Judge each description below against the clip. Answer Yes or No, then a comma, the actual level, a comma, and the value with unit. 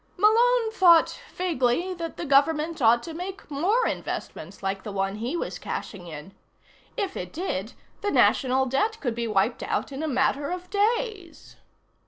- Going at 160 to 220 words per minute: Yes, average, 165 wpm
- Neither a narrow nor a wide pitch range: No, wide, 8.0 semitones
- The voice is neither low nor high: No, very high, 305 Hz